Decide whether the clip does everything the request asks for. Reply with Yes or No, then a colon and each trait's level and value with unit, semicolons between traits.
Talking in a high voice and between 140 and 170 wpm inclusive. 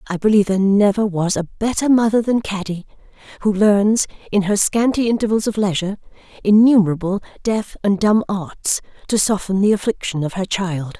Yes: high, 200 Hz; average, 165 wpm